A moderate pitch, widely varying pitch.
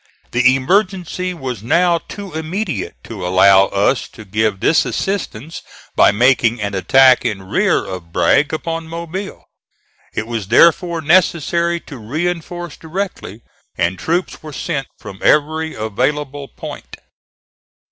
Yes: medium, 145 Hz; wide, 7.5 semitones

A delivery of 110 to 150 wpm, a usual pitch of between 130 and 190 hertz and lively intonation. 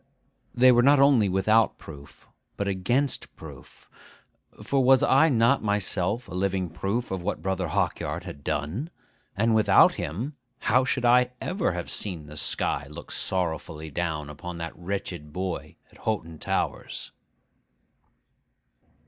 No: average, 140 wpm; very low, 95 Hz; wide, 6.5 semitones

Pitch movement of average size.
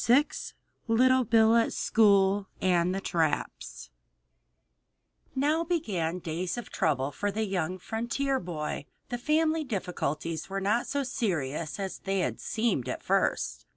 No: wide, 6.0 semitones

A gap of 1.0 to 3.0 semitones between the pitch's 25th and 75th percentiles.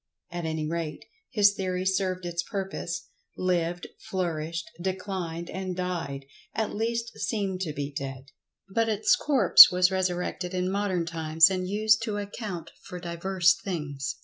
Yes: narrow, 2.6 semitones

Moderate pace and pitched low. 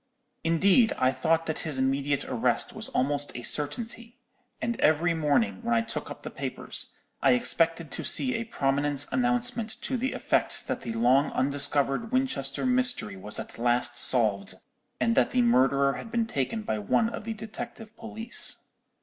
No: average, 165 wpm; medium, 165 Hz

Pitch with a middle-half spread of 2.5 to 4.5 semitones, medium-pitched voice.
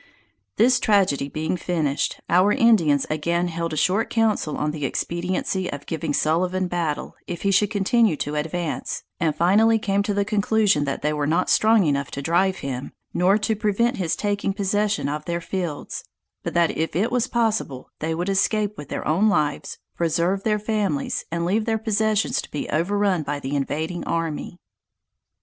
No: average, 5.0 semitones; medium, 180 Hz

